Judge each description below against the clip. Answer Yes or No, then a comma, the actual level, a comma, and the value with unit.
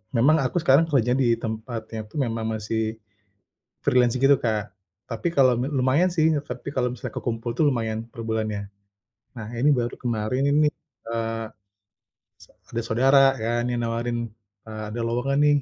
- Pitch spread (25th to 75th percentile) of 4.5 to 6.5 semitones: No, narrow, 2.6 semitones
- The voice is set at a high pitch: No, low, 120 Hz